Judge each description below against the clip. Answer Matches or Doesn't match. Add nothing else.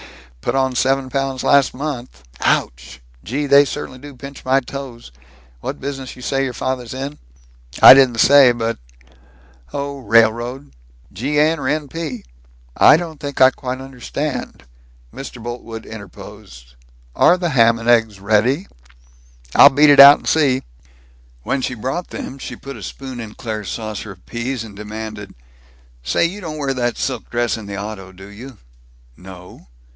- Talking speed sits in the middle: Matches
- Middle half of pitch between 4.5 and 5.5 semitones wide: Doesn't match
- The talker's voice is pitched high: Doesn't match